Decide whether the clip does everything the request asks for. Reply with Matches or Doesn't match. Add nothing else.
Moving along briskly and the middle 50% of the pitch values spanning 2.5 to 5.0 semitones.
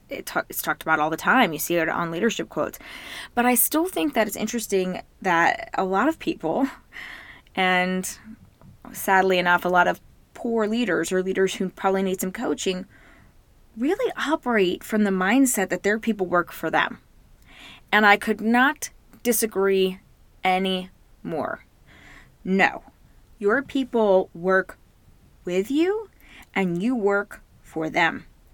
Doesn't match